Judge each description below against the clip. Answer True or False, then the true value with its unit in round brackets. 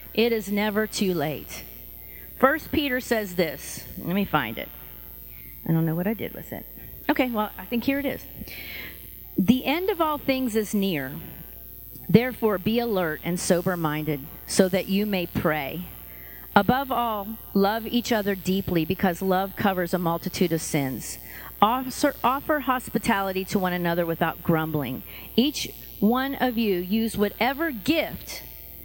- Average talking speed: True (150 wpm)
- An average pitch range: False (6.2 semitones)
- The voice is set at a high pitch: True (195 Hz)